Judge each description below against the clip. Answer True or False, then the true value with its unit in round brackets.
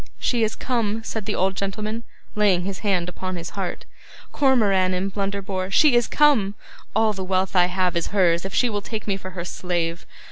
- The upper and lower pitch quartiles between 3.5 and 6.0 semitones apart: False (2.6 semitones)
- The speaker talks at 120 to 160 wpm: False (200 wpm)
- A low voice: False (195 Hz)